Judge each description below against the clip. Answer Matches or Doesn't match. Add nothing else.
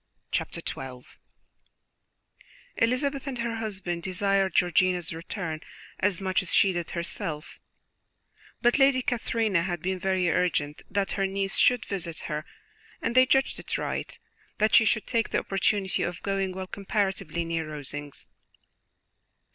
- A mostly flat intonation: Doesn't match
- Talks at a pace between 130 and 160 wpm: Matches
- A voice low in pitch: Doesn't match